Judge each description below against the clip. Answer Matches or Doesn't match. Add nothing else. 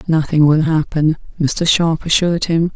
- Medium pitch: Matches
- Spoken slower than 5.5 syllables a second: Matches